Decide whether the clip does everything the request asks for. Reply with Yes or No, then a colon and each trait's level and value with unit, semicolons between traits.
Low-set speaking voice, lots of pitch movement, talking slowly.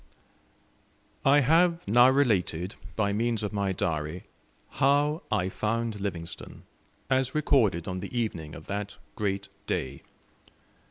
Yes: low, 105 Hz; wide, 6.1 semitones; slow, 120 wpm